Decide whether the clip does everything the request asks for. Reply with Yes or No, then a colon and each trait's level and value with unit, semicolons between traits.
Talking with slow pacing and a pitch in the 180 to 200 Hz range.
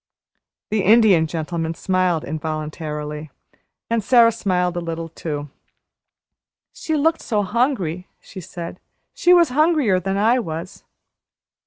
Yes: slow, 120 wpm; medium, 185 Hz